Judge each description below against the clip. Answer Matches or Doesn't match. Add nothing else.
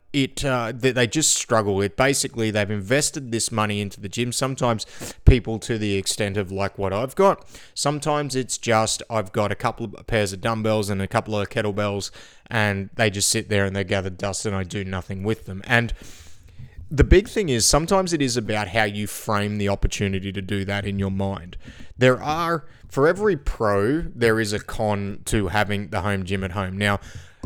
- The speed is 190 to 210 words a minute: Matches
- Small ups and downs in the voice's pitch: Doesn't match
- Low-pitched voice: Matches